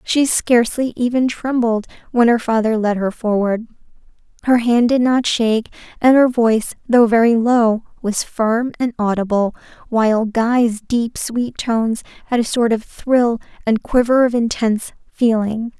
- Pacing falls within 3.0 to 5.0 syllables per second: Yes, 4.5 syllables/s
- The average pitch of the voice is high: Yes, high, 230 Hz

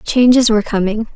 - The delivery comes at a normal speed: Yes, average, 155 wpm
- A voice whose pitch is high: Yes, high, 225 Hz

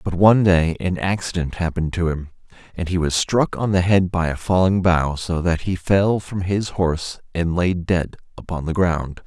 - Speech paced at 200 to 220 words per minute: Yes, fast, 205 wpm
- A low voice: Yes, very low, 90 Hz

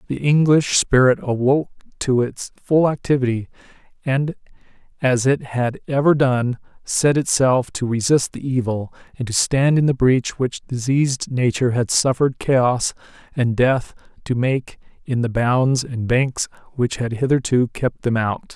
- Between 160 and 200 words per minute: No, average, 150 wpm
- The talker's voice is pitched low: Yes, low, 130 Hz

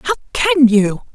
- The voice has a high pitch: Yes, high, 210 Hz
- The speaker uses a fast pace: No, average, 155 wpm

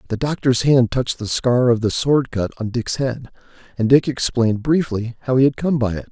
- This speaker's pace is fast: Yes, fast, 225 wpm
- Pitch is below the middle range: Yes, low, 125 Hz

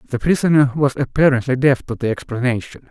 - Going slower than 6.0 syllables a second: No, 6.2 syllables/s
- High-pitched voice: No, low, 130 Hz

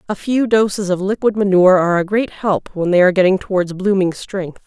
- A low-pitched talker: No, high, 195 Hz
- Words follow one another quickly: Yes, fast, 220 wpm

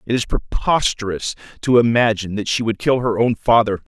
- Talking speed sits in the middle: Yes, average, 185 wpm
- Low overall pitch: Yes, low, 115 Hz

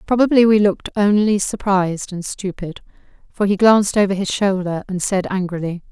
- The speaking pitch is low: No, high, 195 Hz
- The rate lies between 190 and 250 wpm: No, average, 160 wpm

